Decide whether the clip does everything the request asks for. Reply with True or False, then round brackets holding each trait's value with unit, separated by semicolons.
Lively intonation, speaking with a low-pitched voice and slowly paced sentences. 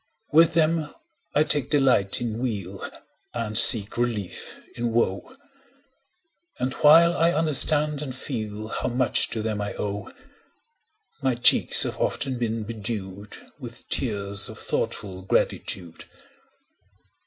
True (6.0 semitones; 120 Hz; 125 wpm)